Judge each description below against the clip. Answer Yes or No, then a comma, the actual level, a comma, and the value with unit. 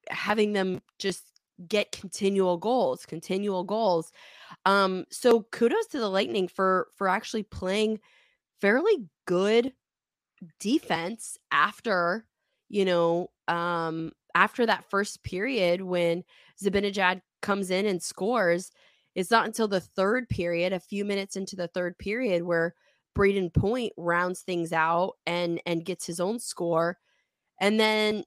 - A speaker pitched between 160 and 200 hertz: Yes, high, 190 Hz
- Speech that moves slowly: Yes, slow, 130 wpm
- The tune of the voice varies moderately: Yes, average, 3.3 semitones